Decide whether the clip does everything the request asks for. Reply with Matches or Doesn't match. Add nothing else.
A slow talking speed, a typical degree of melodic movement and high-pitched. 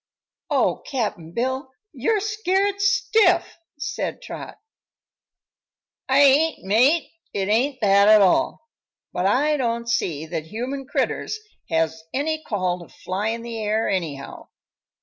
Doesn't match